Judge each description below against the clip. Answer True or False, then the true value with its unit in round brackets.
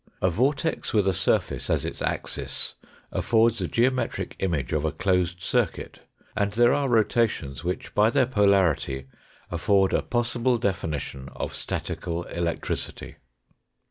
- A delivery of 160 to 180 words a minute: False (135 wpm)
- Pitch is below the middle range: True (100 Hz)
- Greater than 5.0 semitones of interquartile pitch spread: True (5.6 semitones)